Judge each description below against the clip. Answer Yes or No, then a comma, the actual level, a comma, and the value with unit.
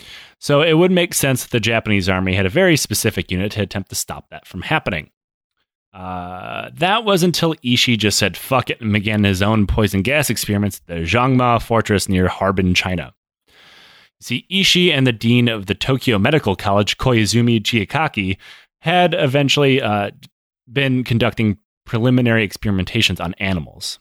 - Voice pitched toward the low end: Yes, low, 115 Hz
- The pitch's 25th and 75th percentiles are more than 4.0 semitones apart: Yes, average, 4.8 semitones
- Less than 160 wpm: No, average, 165 wpm